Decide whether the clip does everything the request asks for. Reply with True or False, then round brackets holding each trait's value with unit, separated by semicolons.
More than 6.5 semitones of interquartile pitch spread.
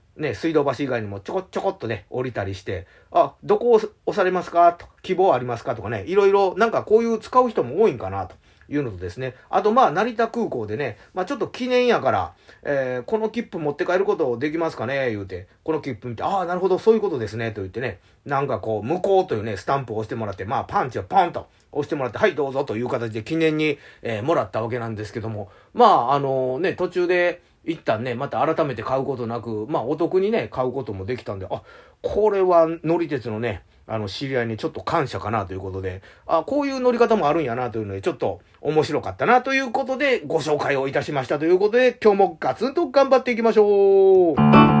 True (8.8 semitones)